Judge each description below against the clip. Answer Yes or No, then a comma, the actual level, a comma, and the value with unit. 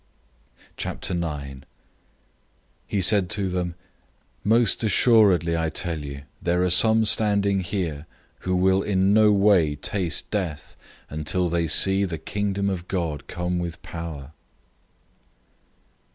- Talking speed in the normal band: No, slow, 120 wpm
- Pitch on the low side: Yes, very low, 90 Hz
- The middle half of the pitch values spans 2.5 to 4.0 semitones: Yes, average, 3.3 semitones